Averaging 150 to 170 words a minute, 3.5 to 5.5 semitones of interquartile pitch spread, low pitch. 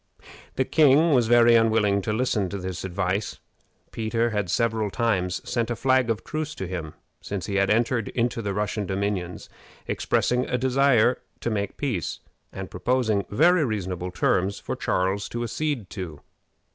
Yes: average, 160 wpm; average, 4.0 semitones; low, 110 Hz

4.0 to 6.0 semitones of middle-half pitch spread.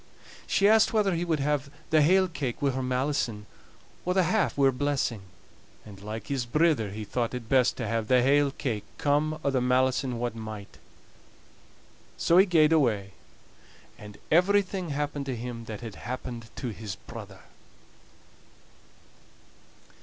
Yes: average, 5.0 semitones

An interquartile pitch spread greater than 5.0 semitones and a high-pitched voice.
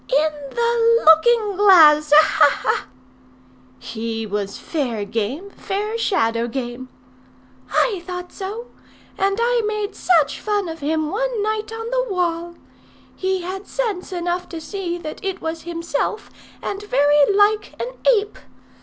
Yes: wide, 5.6 semitones; very high, 360 Hz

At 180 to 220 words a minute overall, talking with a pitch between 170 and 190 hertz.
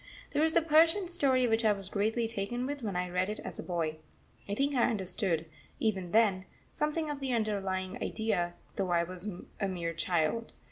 No: average, 195 wpm; high, 210 Hz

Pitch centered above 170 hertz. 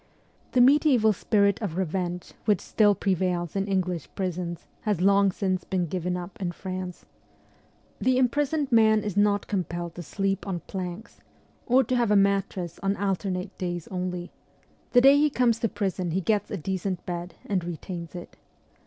Yes: high, 190 Hz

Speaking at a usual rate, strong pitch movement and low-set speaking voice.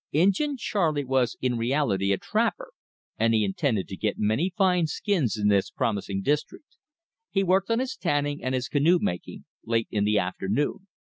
Yes: average, 170 wpm; wide, 9.0 semitones; low, 130 Hz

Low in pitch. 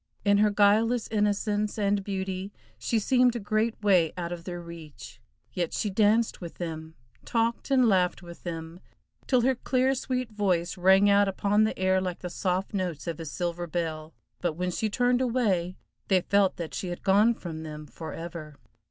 No: high, 190 Hz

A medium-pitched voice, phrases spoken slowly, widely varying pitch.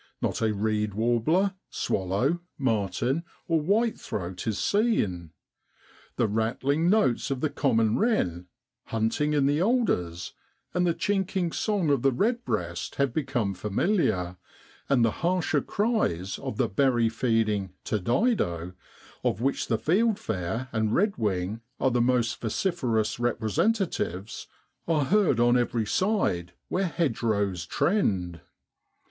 No: low, 120 Hz; slow, 120 wpm; wide, 8.6 semitones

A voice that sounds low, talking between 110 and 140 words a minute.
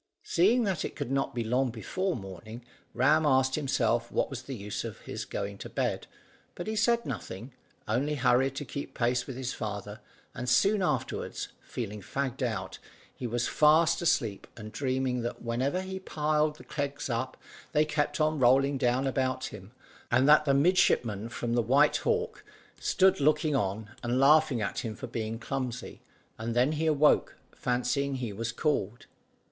No: low, 130 Hz; average, 175 wpm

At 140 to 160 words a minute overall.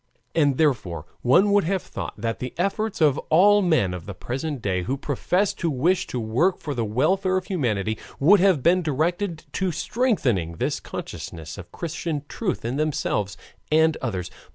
No: average, 175 wpm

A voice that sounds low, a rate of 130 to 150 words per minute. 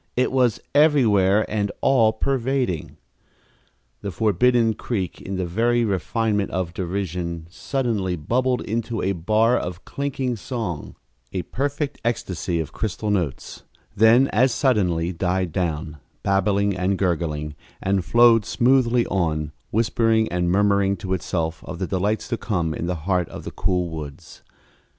Yes: low, 100 Hz; average, 140 wpm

